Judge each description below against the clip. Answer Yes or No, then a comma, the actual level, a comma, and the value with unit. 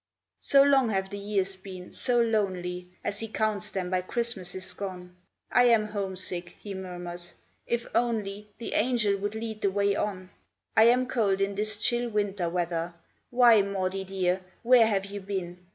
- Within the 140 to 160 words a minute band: No, average, 170 wpm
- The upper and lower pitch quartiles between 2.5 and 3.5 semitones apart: Yes, average, 3.0 semitones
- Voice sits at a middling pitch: No, high, 200 Hz